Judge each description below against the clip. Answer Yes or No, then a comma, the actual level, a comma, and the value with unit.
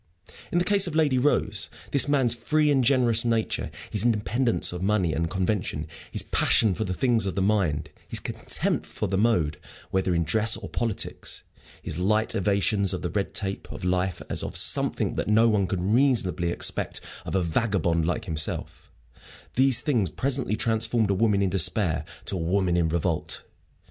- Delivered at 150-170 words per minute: No, average, 180 wpm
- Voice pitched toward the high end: No, low, 105 Hz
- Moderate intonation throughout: Yes, average, 4.5 semitones